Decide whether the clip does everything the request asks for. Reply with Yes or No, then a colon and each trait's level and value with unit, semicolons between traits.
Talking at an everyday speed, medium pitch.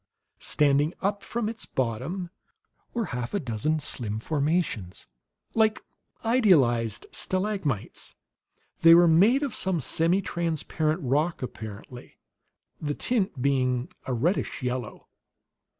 No: slow, 105 wpm; medium, 155 Hz